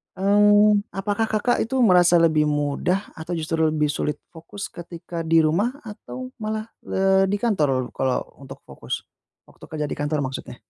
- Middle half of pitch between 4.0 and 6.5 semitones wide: Yes, average, 5.1 semitones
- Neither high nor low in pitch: Yes, medium, 175 Hz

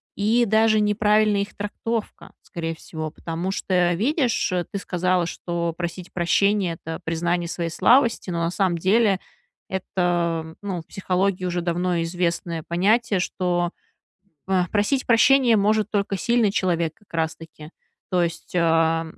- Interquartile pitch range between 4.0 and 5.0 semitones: No, average, 3.5 semitones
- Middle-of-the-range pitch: Yes, medium, 180 Hz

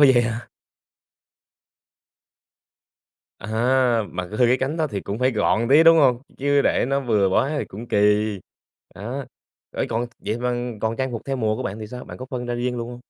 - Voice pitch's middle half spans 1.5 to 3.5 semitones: Yes, average, 3.0 semitones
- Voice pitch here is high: No, low, 120 Hz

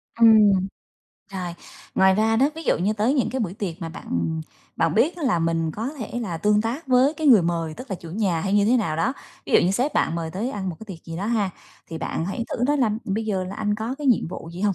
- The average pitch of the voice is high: Yes, high, 205 Hz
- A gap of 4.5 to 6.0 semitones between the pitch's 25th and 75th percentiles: Yes, average, 5.3 semitones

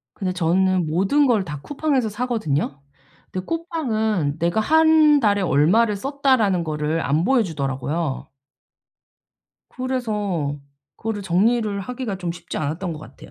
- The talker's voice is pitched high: Yes, high, 195 Hz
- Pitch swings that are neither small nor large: No, wide, 6.9 semitones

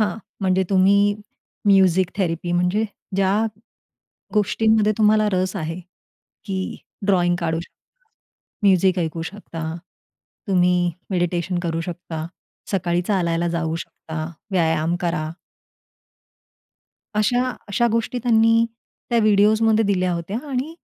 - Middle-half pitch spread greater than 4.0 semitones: No, average, 3.6 semitones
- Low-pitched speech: No, medium, 185 Hz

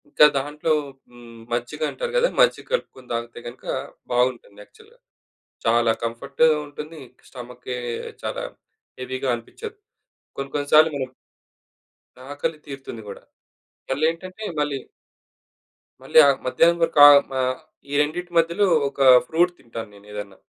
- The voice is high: No, medium, 140 Hz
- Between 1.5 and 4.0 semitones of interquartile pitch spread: No, average, 5.1 semitones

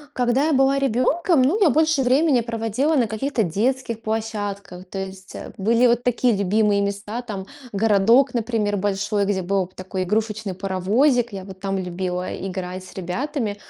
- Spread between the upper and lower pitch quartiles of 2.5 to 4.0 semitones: No, average, 4.4 semitones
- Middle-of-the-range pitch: No, high, 215 Hz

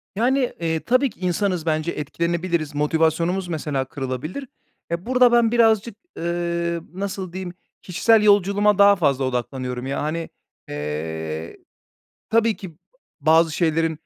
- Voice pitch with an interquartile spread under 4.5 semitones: No, average, 5.0 semitones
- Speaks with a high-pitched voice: No, medium, 170 Hz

